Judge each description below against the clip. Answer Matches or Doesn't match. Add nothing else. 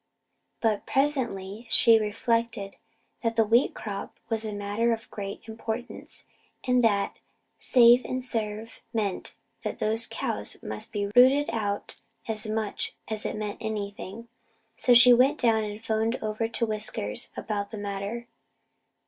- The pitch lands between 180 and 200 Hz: Doesn't match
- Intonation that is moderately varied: Doesn't match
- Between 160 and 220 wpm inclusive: Doesn't match